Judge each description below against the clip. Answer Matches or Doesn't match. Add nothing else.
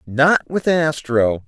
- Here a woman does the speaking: Doesn't match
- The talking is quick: Doesn't match